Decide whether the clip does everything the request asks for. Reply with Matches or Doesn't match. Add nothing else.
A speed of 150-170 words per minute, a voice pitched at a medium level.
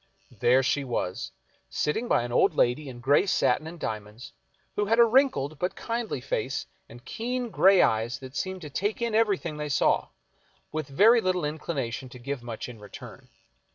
Doesn't match